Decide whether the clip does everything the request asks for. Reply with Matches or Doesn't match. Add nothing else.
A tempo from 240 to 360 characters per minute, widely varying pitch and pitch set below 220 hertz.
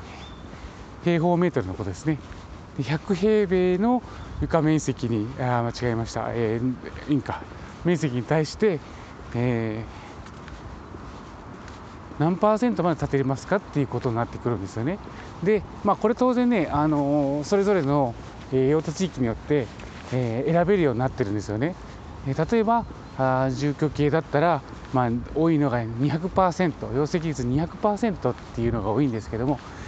Matches